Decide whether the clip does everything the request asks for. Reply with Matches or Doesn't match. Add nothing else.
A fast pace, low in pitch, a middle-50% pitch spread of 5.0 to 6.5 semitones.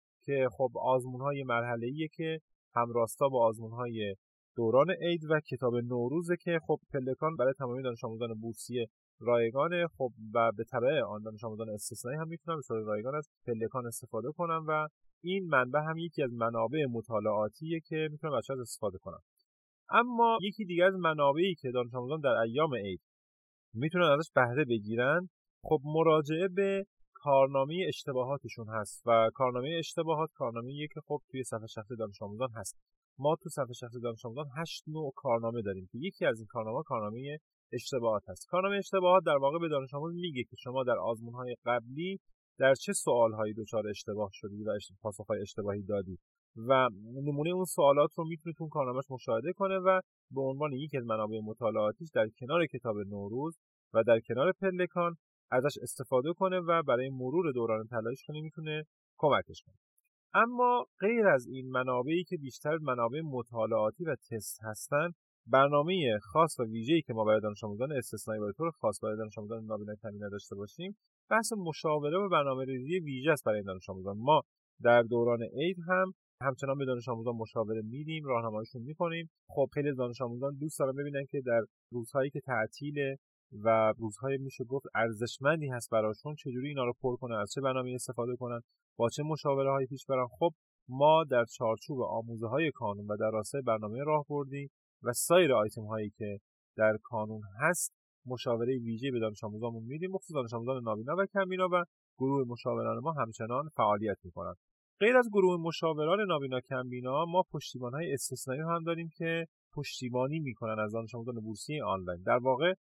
Matches